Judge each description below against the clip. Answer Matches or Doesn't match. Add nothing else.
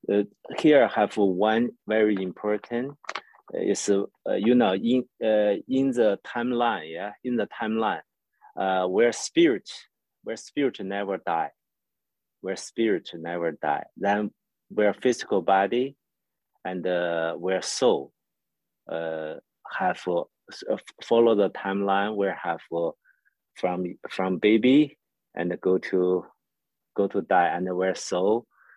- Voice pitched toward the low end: Matches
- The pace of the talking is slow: Matches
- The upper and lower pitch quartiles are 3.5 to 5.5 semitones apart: Matches